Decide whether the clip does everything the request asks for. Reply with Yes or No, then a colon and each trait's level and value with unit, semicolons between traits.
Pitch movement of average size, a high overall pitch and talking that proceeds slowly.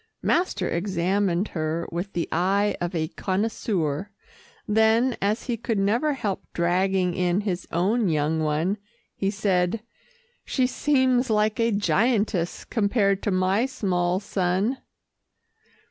Yes: average, 3.8 semitones; high, 195 Hz; slow, 125 wpm